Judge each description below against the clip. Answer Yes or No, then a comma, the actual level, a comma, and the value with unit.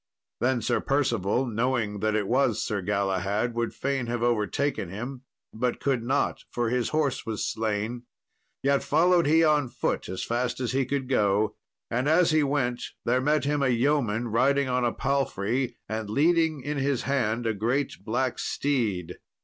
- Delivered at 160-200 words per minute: Yes, average, 170 wpm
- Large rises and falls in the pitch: No, average, 4.0 semitones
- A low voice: Yes, low, 125 Hz